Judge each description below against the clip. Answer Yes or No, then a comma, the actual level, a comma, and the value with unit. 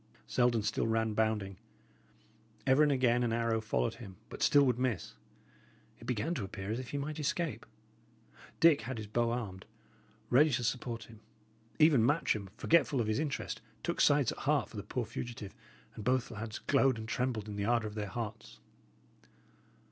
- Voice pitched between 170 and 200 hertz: No, low, 115 Hz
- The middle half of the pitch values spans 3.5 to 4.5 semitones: No, average, 3.1 semitones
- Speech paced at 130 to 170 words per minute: No, average, 180 wpm